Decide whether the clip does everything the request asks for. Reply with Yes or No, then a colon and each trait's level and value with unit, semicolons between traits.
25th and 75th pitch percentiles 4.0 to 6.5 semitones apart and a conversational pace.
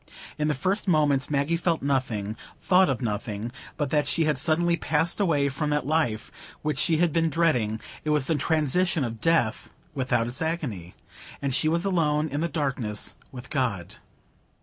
Yes: average, 4.4 semitones; average, 170 wpm